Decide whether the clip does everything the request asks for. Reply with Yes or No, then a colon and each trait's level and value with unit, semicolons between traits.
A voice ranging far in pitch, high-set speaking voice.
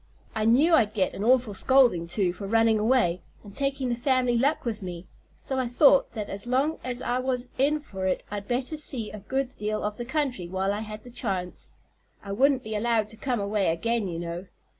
No: average, 4.3 semitones; high, 225 Hz